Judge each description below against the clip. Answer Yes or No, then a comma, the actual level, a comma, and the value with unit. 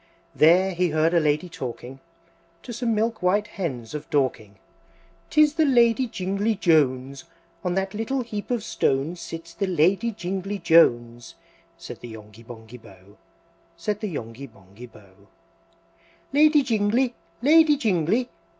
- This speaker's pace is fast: No, average, 140 wpm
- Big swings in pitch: Yes, wide, 8.6 semitones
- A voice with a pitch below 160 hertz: No, medium, 170 Hz